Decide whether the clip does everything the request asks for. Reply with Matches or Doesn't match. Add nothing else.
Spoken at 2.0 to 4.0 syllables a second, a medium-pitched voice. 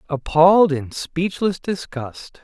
Matches